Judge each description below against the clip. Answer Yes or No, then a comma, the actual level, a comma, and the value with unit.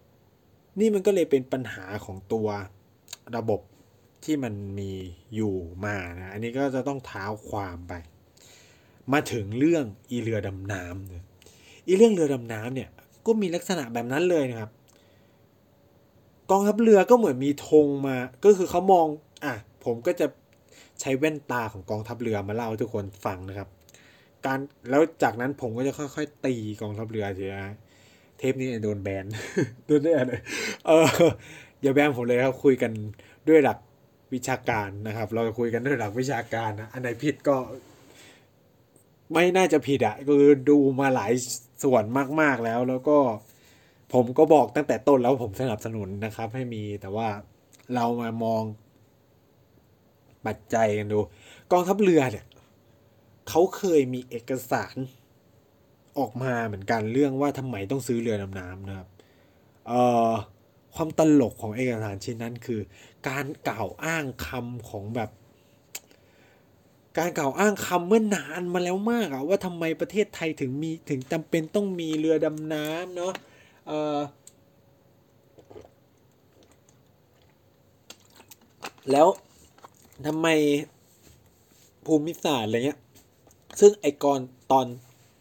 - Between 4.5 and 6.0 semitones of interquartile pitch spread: Yes, average, 5.2 semitones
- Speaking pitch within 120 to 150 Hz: Yes, low, 125 Hz